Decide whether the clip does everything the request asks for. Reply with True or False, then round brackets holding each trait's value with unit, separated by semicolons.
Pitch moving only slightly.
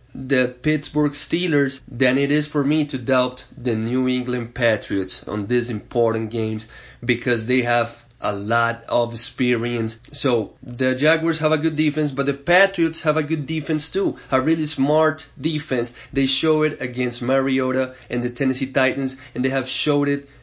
False (3.5 semitones)